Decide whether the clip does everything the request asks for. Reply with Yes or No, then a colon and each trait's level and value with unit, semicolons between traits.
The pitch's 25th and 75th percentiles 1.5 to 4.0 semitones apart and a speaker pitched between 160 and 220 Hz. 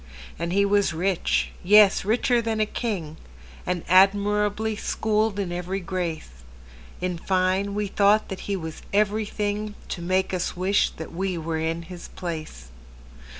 Yes: average, 3.4 semitones; high, 190 Hz